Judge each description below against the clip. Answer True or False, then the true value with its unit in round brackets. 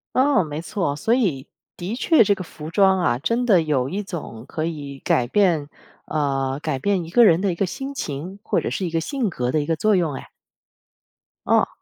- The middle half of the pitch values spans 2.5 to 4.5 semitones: False (5.6 semitones)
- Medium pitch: True (170 Hz)